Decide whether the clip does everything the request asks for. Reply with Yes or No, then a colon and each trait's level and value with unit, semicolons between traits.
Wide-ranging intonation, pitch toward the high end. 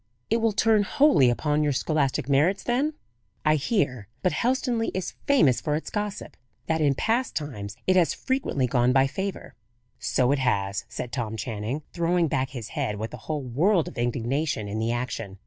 No: wide, 7.8 semitones; medium, 145 Hz